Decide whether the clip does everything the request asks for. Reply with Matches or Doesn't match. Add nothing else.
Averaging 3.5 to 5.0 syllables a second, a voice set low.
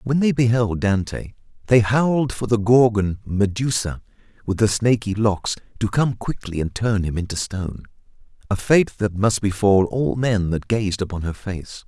Matches